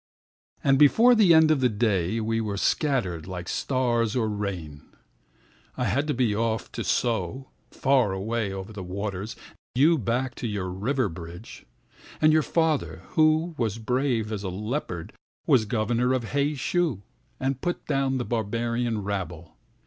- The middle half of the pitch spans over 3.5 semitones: Yes, average, 5.1 semitones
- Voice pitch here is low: Yes, low, 115 Hz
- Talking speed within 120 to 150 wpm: Yes, average, 145 wpm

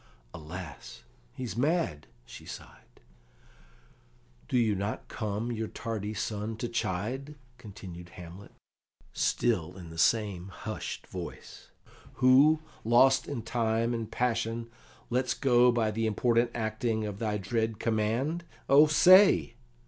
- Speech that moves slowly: Yes, slow, 120 wpm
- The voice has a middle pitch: No, low, 115 Hz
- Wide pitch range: No, average, 3.0 semitones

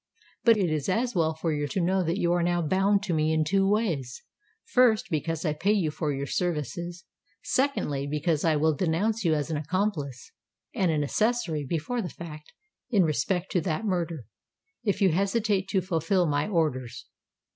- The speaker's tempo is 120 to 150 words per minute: No, average, 180 wpm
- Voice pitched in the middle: Yes, medium, 170 Hz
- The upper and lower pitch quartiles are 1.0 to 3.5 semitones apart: No, average, 4.2 semitones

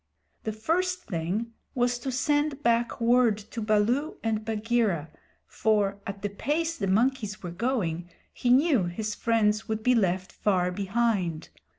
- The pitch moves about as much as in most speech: Yes, average, 3.8 semitones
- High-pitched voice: Yes, high, 220 Hz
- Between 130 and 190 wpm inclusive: Yes, average, 150 wpm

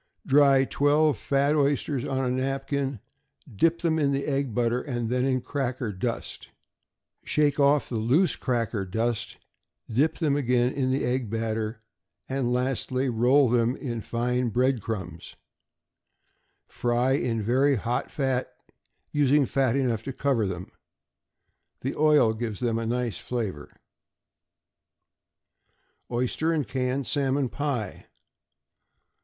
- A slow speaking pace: Yes, slow, 125 wpm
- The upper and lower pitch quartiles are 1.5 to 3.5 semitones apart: Yes, average, 3.0 semitones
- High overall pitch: No, low, 125 Hz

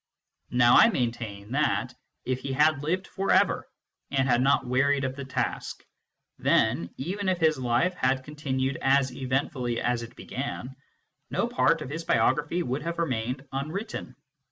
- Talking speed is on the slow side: No, average, 155 wpm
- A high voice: No, low, 135 Hz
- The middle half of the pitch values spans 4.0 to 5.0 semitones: No, average, 3.3 semitones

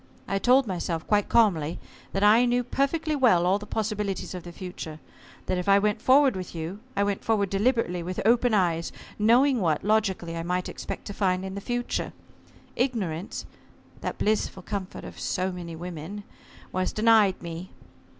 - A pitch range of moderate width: Yes, average, 3.8 semitones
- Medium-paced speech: Yes, average, 170 wpm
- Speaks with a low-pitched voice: No, high, 195 Hz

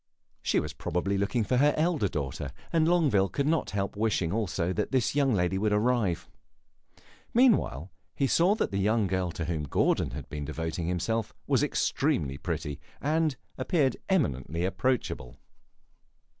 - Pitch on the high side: No, low, 100 Hz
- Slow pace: No, average, 155 wpm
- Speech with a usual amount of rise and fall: No, wide, 8.1 semitones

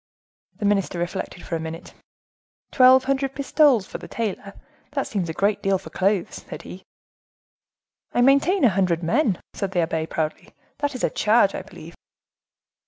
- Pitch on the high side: Yes, high, 200 Hz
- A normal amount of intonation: No, wide, 6.4 semitones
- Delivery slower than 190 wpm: Yes, average, 170 wpm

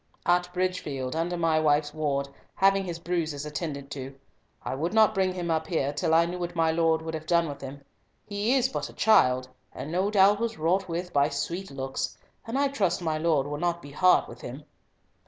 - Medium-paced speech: No, fast, 210 wpm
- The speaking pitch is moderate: Yes, medium, 165 Hz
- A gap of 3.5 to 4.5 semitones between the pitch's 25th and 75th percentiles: Yes, average, 3.9 semitones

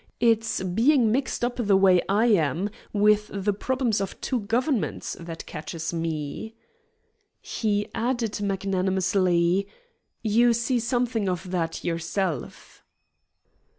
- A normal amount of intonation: Yes, average, 4.1 semitones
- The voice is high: Yes, high, 205 Hz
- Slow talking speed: Yes, slow, 115 wpm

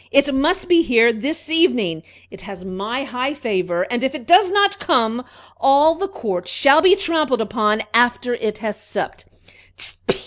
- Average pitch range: No, wide, 6.9 semitones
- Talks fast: No, average, 165 wpm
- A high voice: Yes, very high, 250 Hz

